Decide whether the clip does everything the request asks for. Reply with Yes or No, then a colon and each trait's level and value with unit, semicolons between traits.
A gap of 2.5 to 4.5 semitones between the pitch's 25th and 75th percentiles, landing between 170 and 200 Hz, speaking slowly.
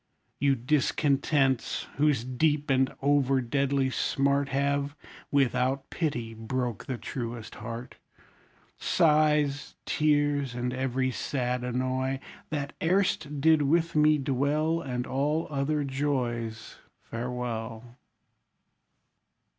No: average, 2.8 semitones; low, 135 Hz; slow, 100 wpm